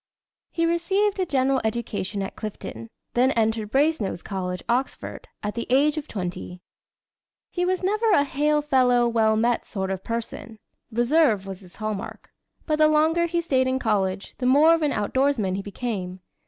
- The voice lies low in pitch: No, high, 245 Hz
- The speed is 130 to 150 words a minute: No, average, 165 wpm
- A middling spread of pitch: No, wide, 6.6 semitones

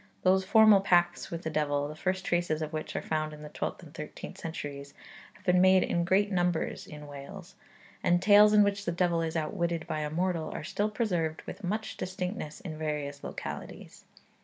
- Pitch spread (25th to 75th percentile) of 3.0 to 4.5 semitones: Yes, average, 3.4 semitones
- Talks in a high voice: No, medium, 170 Hz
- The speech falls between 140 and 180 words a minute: No, average, 195 wpm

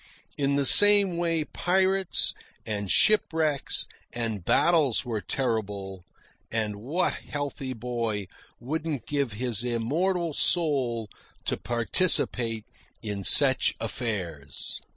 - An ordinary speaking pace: No, slow, 100 wpm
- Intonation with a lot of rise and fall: Yes, wide, 6.4 semitones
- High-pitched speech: No, low, 125 Hz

